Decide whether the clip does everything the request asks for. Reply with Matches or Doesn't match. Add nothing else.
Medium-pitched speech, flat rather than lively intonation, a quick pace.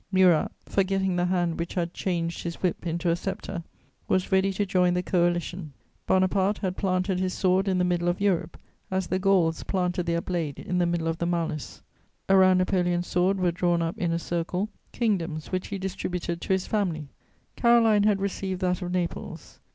Doesn't match